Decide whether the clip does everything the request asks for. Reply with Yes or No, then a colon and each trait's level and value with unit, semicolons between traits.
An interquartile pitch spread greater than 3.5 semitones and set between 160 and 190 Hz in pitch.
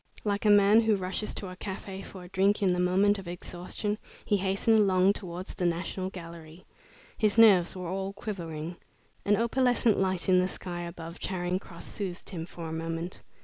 No: narrow, 2.6 semitones; medium, 185 Hz